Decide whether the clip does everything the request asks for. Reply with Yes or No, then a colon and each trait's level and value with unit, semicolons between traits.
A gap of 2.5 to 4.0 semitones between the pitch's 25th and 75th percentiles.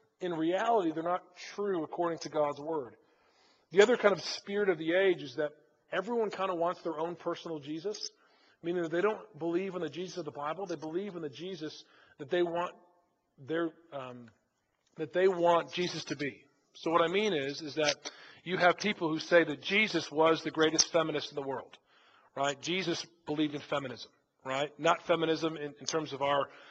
Yes: average, 2.9 semitones